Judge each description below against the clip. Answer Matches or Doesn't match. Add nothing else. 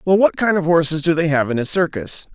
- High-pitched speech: Doesn't match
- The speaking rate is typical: Doesn't match